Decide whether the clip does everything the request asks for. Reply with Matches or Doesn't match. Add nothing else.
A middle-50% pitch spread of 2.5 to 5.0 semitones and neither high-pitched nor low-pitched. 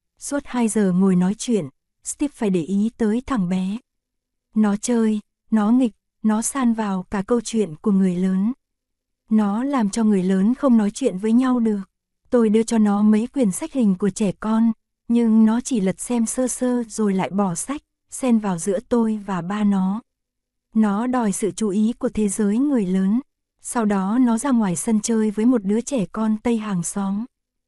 Doesn't match